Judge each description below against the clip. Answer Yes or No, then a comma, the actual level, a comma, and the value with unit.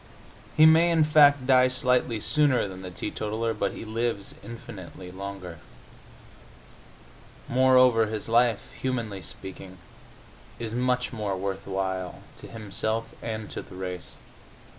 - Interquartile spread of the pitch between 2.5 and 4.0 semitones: No, average, 4.6 semitones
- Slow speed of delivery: Yes, slow, 125 wpm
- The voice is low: Yes, low, 115 Hz